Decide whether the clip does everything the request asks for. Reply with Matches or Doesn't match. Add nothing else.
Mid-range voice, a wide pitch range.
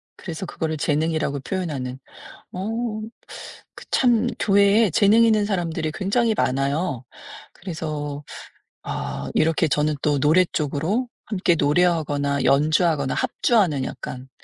Doesn't match